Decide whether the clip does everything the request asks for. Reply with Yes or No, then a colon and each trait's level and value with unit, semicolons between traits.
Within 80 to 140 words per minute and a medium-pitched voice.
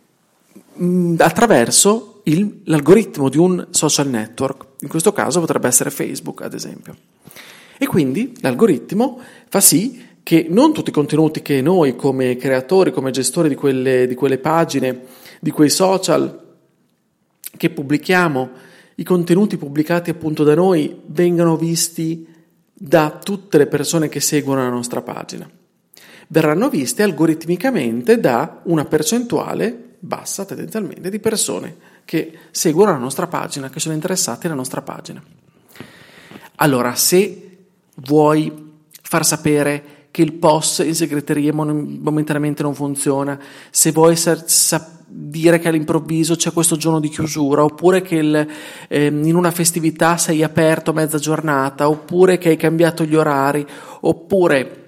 Yes: average, 135 wpm; medium, 160 Hz